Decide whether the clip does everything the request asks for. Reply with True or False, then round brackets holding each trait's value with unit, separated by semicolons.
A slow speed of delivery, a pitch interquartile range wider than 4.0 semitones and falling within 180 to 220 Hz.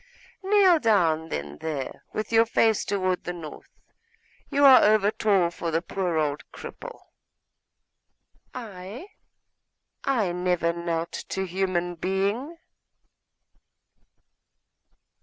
True (100 wpm; 4.8 semitones; 185 Hz)